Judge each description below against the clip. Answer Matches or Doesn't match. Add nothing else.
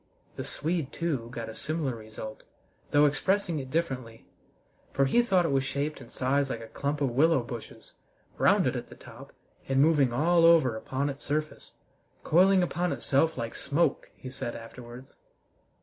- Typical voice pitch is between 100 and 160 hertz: Matches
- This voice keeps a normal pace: Matches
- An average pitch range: Matches